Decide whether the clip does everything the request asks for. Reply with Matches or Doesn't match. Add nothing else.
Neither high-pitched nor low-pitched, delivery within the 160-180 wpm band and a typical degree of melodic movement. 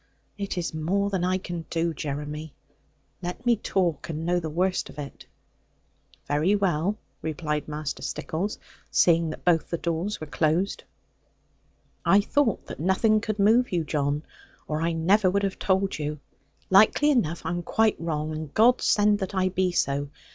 Matches